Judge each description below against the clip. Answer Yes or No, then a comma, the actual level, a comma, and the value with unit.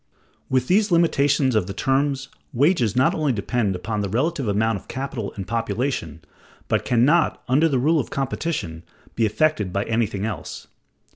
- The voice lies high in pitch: No, low, 125 Hz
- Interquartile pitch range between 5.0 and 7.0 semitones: Yes, average, 5.3 semitones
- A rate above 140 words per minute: Yes, average, 165 wpm